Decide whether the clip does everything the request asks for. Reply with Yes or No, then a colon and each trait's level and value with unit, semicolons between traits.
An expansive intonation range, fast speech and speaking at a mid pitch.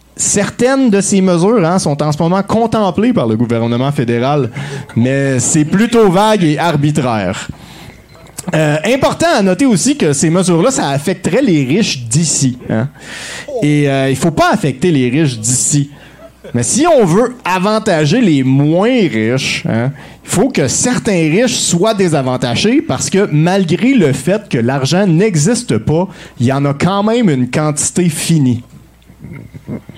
No: wide, 6.8 semitones; average, 155 wpm; medium, 160 Hz